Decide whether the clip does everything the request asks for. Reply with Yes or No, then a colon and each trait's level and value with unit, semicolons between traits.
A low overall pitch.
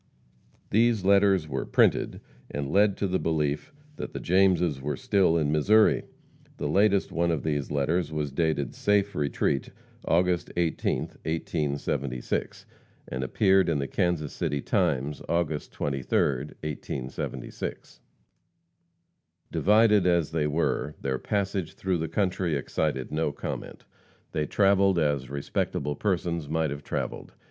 Yes: very low, 80 Hz